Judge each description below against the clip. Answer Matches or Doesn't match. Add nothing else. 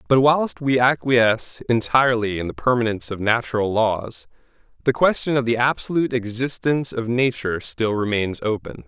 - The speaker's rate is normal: Matches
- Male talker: Matches